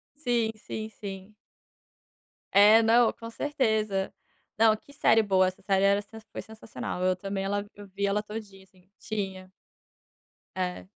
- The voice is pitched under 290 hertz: Yes, high, 205 Hz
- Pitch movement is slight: Yes, narrow, 2.3 semitones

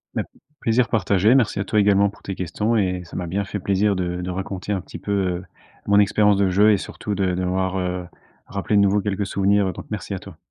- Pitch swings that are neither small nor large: No, narrow, 1.8 semitones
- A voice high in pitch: No, low, 100 Hz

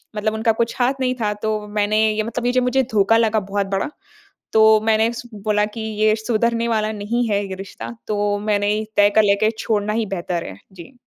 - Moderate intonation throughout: No, narrow, 2.0 semitones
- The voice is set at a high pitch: Yes, high, 215 Hz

